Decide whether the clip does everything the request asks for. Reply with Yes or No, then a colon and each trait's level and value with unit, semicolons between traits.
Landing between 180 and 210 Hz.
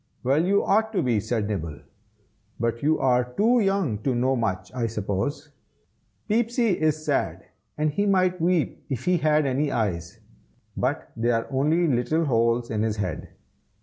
No: low, 135 Hz